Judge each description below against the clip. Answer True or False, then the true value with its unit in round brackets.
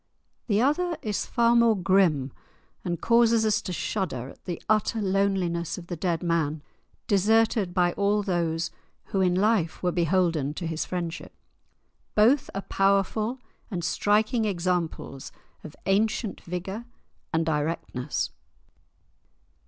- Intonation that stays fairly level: False (4.2 semitones)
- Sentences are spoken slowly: True (130 wpm)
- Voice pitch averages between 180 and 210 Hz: True (190 Hz)